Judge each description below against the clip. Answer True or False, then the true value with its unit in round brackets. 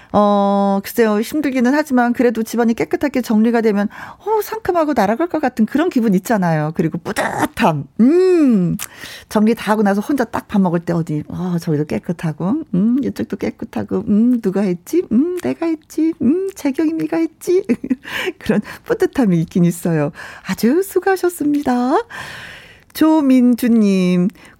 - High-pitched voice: True (240 Hz)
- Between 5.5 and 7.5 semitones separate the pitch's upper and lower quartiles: False (8.0 semitones)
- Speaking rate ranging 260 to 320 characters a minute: True (310 characters per minute)